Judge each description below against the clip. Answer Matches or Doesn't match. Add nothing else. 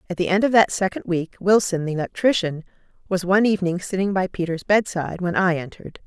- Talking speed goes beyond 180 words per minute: Matches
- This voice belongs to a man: Doesn't match